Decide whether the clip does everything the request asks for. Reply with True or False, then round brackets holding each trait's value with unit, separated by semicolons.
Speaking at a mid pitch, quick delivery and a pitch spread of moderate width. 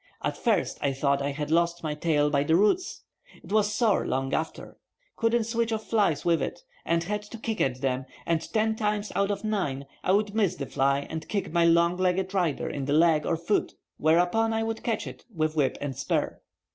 False (170 Hz; 210 wpm; 6.1 semitones)